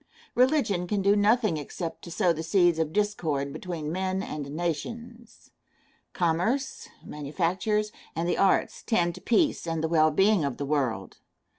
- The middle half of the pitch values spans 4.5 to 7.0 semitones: Yes, average, 4.8 semitones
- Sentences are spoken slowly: No, average, 155 wpm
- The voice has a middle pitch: Yes, medium, 175 Hz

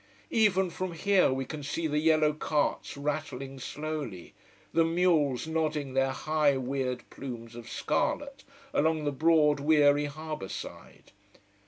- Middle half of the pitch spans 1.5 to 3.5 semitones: Yes, average, 2.8 semitones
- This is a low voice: No, medium, 150 Hz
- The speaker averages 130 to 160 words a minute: Yes, slow, 135 wpm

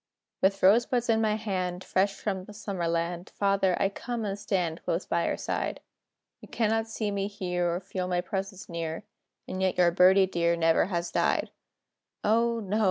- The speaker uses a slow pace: No, average, 185 wpm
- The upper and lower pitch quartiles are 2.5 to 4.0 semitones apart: Yes, average, 2.9 semitones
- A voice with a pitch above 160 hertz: Yes, high, 190 Hz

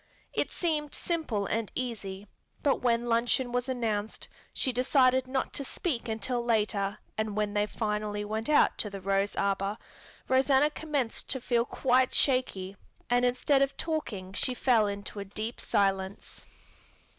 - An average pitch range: Yes, average, 3.9 semitones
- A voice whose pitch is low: No, high, 235 Hz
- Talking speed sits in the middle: Yes, average, 150 wpm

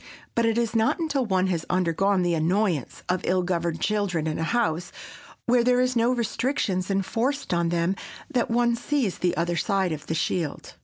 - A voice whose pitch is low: No, high, 190 Hz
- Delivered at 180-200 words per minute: Yes, average, 190 wpm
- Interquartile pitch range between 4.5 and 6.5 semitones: Yes, wide, 5.4 semitones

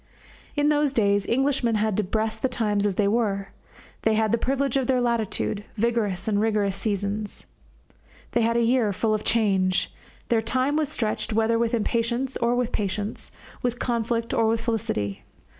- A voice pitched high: Yes, high, 225 Hz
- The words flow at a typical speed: Yes, average, 175 wpm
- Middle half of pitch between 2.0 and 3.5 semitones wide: Yes, narrow, 2.4 semitones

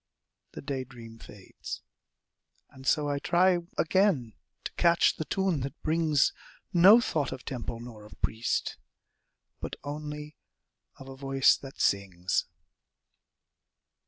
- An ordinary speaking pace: No, slow, 125 wpm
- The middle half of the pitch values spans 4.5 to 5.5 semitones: Yes, average, 4.9 semitones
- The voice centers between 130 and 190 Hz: Yes, medium, 140 Hz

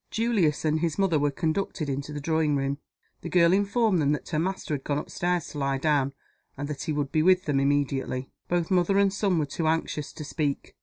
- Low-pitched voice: No, medium, 155 Hz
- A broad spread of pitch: No, average, 3.7 semitones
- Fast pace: Yes, fast, 225 wpm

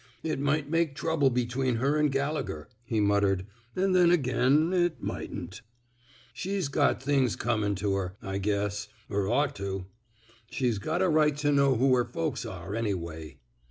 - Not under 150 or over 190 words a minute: Yes, average, 170 wpm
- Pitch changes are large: Yes, wide, 6.6 semitones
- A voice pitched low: Yes, low, 125 Hz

